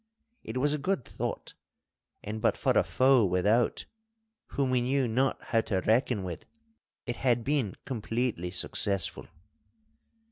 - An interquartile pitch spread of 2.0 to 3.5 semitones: No, average, 3.9 semitones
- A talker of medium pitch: No, low, 120 Hz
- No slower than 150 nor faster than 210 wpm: No, average, 140 wpm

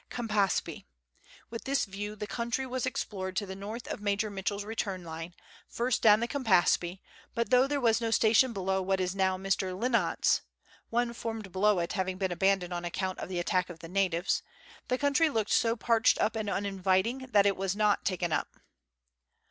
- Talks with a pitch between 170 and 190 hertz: No, high, 200 Hz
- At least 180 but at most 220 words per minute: Yes, average, 190 wpm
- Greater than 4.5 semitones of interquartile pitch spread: No, average, 3.5 semitones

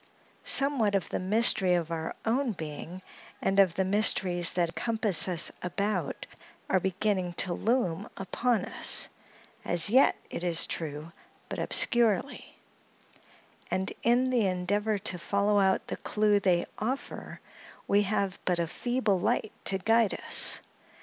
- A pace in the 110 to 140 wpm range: Yes, slow, 135 wpm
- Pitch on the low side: No, high, 195 Hz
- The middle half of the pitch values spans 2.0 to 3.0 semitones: No, average, 3.5 semitones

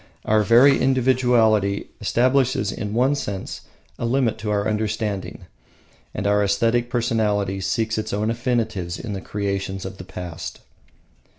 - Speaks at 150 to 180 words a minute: No, slow, 135 wpm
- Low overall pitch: Yes, low, 110 Hz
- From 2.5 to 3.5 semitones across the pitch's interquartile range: Yes, average, 3.2 semitones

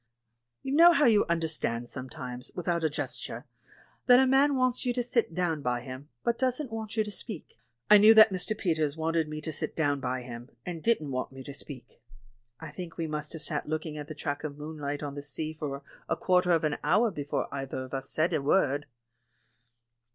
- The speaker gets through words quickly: Yes, fast, 210 wpm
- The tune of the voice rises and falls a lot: Yes, wide, 6.4 semitones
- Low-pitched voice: No, medium, 155 Hz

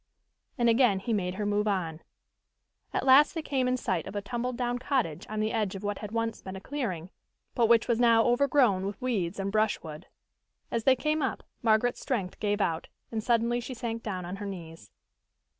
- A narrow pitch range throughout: No, average, 4.0 semitones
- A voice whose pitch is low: No, high, 220 Hz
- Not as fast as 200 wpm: No, fast, 205 wpm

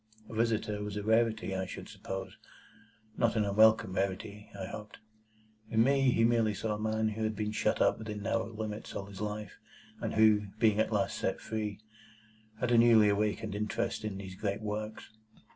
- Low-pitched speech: Yes, low, 105 Hz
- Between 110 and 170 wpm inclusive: No, average, 185 wpm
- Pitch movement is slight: Yes, narrow, 1.3 semitones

